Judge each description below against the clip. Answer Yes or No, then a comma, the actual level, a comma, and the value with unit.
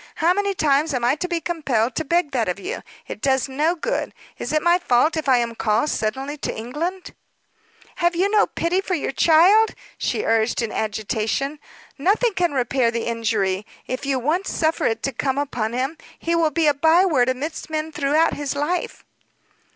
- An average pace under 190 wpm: No, average, 195 wpm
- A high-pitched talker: Yes, very high, 290 Hz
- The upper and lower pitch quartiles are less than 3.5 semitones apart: No, wide, 5.5 semitones